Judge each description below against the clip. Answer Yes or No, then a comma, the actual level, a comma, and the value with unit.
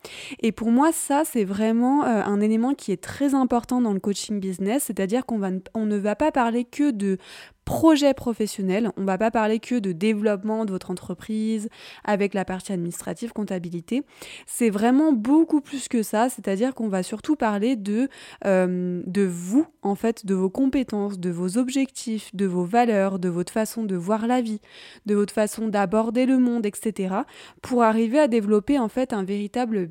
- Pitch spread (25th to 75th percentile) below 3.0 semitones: No, average, 3.9 semitones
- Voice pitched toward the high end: Yes, high, 220 Hz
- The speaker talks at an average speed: Yes, average, 190 wpm